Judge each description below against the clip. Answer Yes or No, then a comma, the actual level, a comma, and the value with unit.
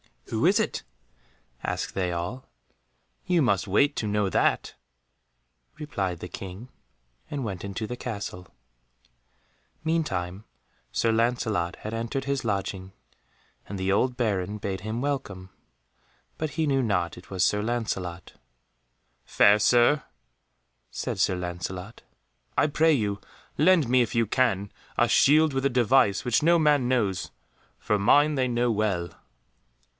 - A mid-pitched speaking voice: No, low, 110 Hz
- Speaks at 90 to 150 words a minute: Yes, average, 140 wpm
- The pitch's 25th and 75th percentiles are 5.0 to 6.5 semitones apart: Yes, wide, 5.6 semitones